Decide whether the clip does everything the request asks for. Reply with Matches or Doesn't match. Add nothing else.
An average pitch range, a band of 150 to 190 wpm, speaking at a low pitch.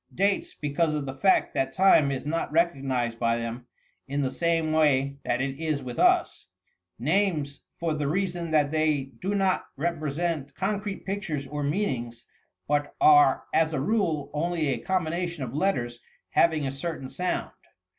Doesn't match